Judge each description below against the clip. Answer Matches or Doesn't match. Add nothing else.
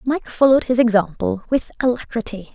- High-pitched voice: Matches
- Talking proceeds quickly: Doesn't match